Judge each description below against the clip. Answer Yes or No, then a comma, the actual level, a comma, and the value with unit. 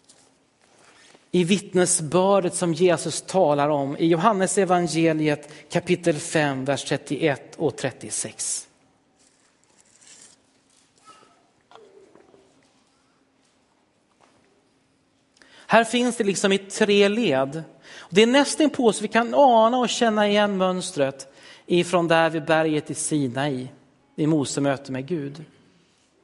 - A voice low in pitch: No, medium, 175 Hz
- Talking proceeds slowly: Yes, slow, 105 wpm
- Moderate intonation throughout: No, wide, 5.9 semitones